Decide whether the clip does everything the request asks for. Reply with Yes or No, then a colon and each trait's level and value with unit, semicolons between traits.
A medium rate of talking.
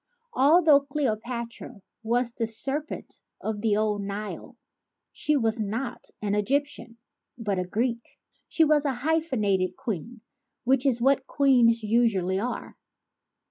No: slow, 125 wpm